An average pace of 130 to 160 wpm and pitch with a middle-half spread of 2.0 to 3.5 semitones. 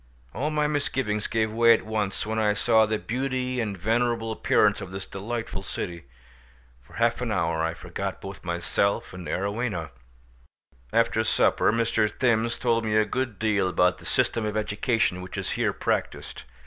No: average, 170 wpm; average, 3.2 semitones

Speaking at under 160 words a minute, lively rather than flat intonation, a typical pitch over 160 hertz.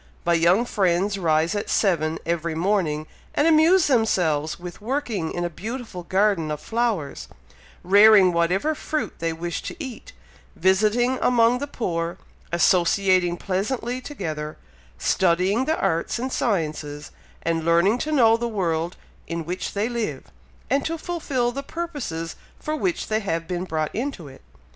Yes: average, 150 wpm; wide, 6.3 semitones; high, 190 Hz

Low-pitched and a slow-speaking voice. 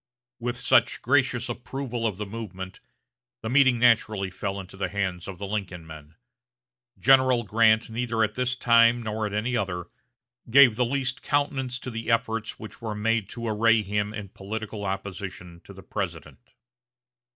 No: low, 110 Hz; average, 160 wpm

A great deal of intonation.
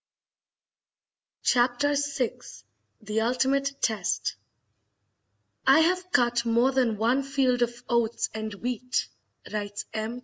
No: average, 3.1 semitones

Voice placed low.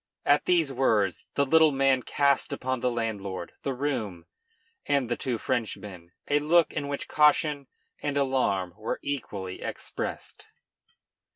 Yes: low, 130 Hz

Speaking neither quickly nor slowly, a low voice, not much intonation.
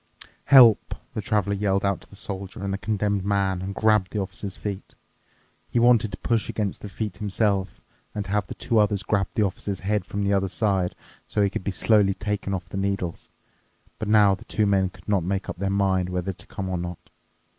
No: fast, 215 wpm; low, 100 Hz; narrow, 1.5 semitones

